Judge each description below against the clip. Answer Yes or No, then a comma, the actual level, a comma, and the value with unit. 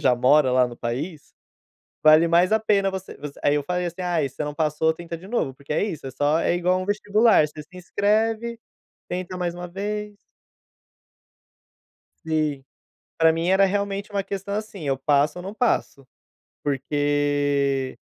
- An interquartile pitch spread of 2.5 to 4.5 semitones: No, average, 5.3 semitones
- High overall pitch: No, medium, 170 Hz